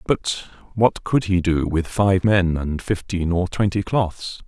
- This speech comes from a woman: No, male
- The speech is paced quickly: No, average, 175 wpm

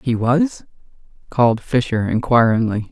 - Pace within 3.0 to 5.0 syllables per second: Yes, 4.5 syllables/s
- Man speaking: Yes, male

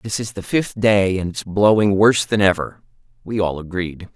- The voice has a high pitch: No, low, 100 Hz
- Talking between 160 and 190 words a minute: No, average, 200 wpm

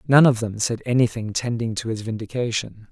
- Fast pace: No, average, 185 wpm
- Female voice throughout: No, male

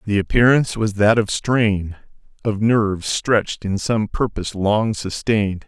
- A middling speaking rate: Yes, average, 150 wpm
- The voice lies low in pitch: Yes, low, 105 Hz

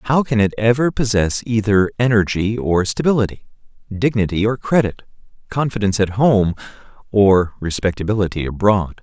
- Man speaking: Yes, male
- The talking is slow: Yes, slow, 120 wpm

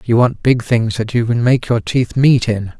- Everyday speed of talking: No, fast, 260 wpm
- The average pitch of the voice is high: No, low, 120 Hz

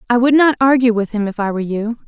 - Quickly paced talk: Yes, fast, 290 wpm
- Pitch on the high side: Yes, high, 230 Hz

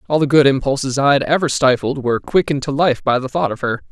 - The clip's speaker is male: Yes, male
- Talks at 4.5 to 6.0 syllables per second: No, 6.5 syllables/s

